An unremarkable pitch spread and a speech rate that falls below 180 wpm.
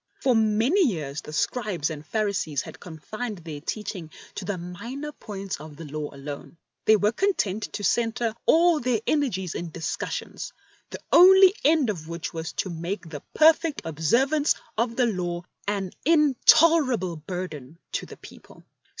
No: wide, 7.5 semitones; average, 160 wpm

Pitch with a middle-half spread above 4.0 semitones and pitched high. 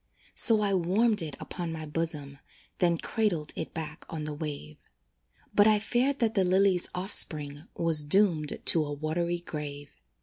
No: average, 4.5 semitones; medium, 165 Hz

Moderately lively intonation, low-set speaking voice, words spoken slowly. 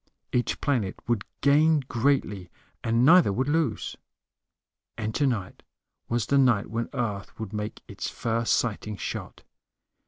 Yes: average, 4.5 semitones; low, 115 Hz; slow, 130 wpm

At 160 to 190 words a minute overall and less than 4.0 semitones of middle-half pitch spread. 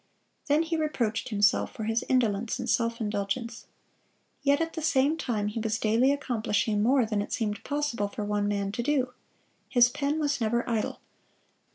No: average, 175 wpm; average, 4.8 semitones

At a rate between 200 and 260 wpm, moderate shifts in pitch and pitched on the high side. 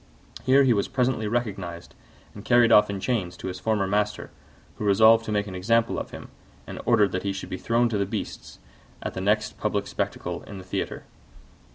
No: fast, 205 wpm; average, 3.1 semitones; low, 105 Hz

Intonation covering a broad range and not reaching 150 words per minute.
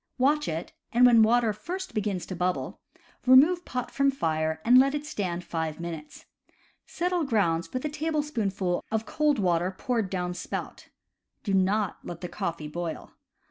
No: wide, 7.5 semitones; average, 160 wpm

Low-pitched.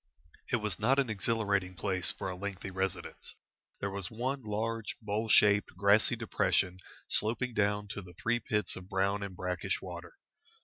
Yes: low, 105 Hz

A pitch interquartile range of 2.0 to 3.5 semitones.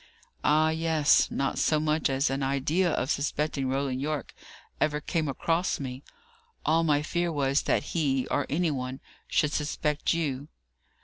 Yes: narrow, 2.5 semitones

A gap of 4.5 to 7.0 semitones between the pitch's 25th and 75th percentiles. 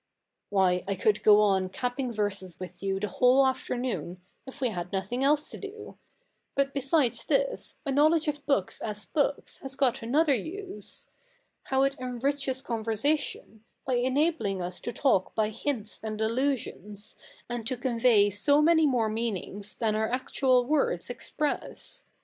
Yes: average, 5.0 semitones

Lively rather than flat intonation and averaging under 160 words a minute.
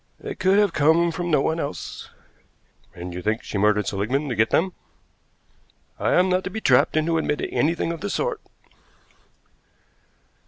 No: wide, 8.2 semitones; average, 165 wpm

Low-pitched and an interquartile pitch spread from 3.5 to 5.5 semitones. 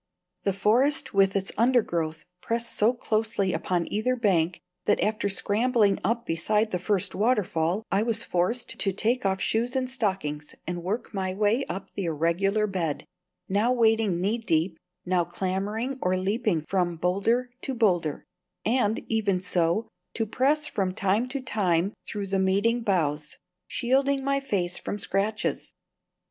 No: high, 200 Hz; average, 4.1 semitones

